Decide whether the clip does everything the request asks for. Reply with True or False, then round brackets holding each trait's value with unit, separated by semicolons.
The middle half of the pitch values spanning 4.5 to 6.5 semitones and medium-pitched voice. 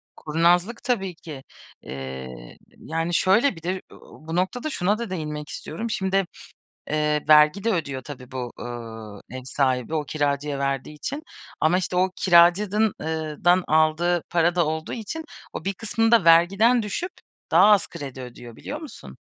True (5.0 semitones; 165 Hz)